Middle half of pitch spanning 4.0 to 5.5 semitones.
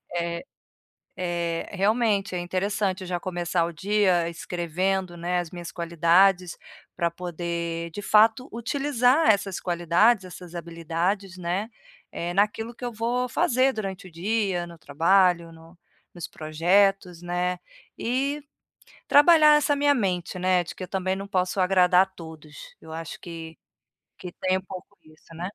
No: average, 3.1 semitones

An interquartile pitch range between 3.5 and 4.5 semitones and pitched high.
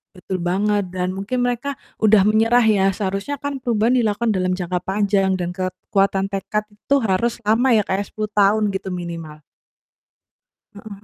No: average, 2.7 semitones; high, 205 Hz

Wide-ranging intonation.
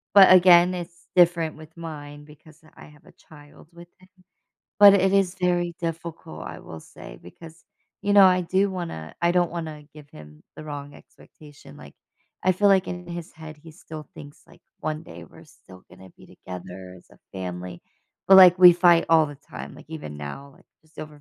No: average, 3.4 semitones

